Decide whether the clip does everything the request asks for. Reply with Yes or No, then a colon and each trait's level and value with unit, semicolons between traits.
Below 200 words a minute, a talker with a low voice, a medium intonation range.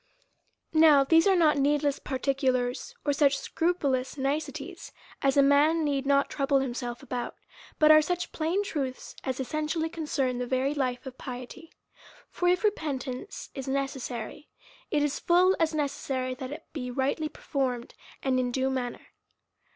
No: average, 155 wpm; very high, 280 Hz; average, 3.1 semitones